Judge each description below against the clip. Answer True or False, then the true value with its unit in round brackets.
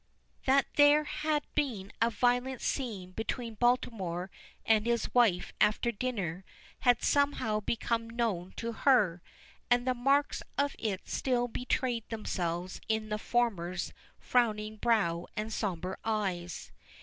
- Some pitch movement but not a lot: True (4.1 semitones)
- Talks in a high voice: True (230 Hz)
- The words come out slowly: True (125 wpm)